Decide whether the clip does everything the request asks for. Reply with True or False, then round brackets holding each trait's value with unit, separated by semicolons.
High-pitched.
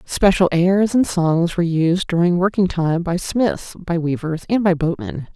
False (175 Hz)